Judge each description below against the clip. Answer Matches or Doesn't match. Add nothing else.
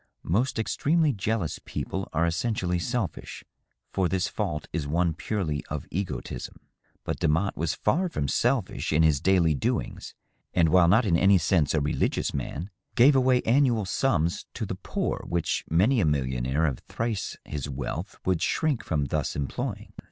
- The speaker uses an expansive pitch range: Matches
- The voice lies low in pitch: Matches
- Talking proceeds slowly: Doesn't match